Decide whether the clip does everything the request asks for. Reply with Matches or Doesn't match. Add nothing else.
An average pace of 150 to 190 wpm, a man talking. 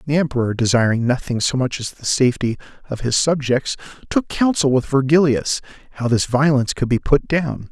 Matches